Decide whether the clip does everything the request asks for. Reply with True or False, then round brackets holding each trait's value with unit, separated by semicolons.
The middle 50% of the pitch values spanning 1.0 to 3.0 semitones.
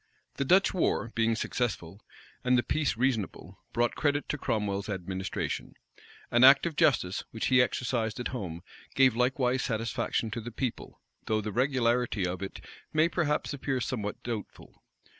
False (3.7 semitones)